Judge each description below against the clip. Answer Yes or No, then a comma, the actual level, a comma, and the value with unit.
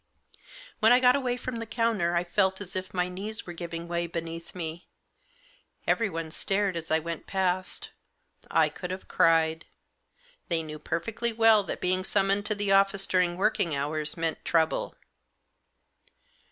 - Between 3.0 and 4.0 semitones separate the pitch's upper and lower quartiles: Yes, average, 3.6 semitones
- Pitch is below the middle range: No, medium, 185 Hz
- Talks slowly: No, average, 160 wpm